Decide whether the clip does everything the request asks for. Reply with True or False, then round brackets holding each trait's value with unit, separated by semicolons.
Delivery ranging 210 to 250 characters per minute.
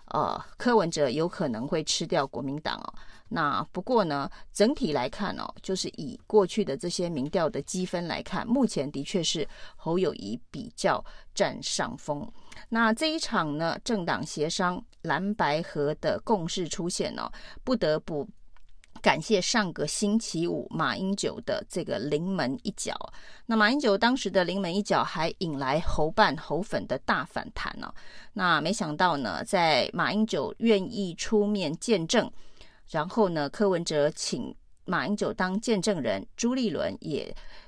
True (235 characters per minute)